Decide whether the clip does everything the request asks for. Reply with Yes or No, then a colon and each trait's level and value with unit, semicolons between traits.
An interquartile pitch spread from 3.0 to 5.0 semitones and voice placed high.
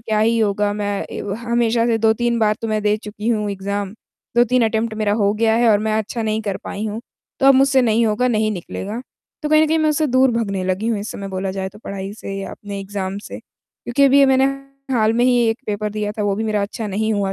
No: narrow, 2.5 semitones; high, 215 Hz